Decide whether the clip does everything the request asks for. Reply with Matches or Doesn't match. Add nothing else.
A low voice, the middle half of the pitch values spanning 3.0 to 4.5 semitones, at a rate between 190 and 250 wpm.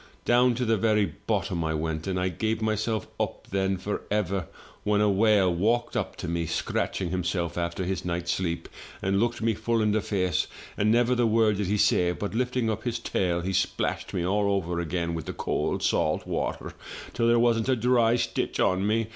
Matches